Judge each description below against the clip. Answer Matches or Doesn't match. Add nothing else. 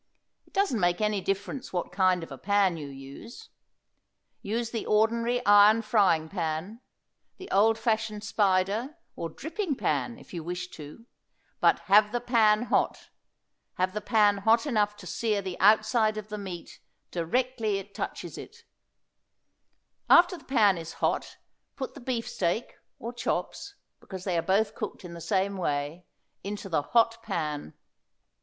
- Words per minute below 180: Matches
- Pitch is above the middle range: Matches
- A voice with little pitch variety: Doesn't match